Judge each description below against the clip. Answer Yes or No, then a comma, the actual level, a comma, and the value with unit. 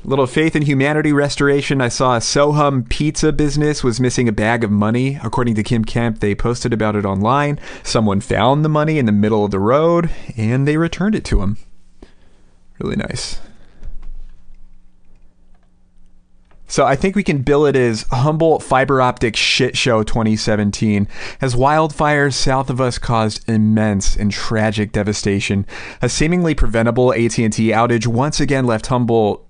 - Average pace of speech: Yes, average, 160 wpm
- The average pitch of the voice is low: Yes, low, 120 Hz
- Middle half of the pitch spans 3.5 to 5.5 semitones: Yes, average, 4.9 semitones